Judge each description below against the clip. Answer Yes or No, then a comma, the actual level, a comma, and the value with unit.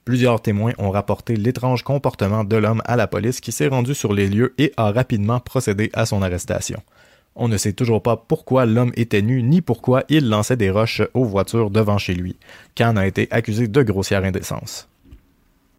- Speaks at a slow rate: No, average, 195 wpm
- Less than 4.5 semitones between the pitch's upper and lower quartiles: Yes, average, 3.5 semitones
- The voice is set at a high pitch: No, low, 115 Hz